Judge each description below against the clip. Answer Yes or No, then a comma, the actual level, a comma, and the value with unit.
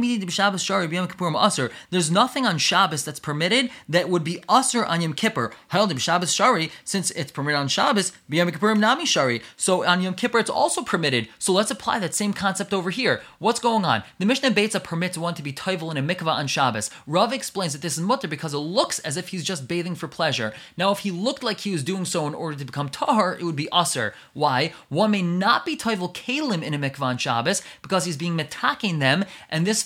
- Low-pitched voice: No, medium, 180 Hz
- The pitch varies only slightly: No, average, 4.1 semitones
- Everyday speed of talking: No, fast, 210 wpm